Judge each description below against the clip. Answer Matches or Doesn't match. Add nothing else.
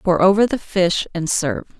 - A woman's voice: Matches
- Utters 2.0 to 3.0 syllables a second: Doesn't match